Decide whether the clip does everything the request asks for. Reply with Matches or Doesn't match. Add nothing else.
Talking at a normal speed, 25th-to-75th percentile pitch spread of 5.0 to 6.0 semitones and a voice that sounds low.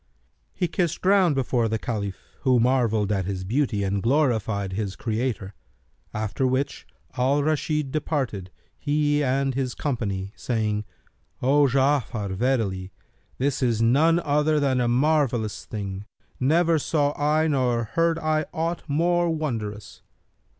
Doesn't match